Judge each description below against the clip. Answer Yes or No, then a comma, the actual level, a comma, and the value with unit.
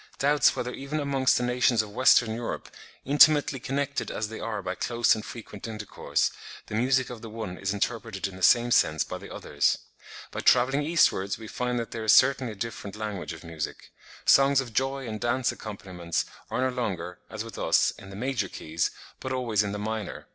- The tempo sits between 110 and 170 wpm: No, average, 200 wpm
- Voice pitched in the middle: No, low, 115 Hz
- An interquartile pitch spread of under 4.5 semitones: Yes, average, 3.9 semitones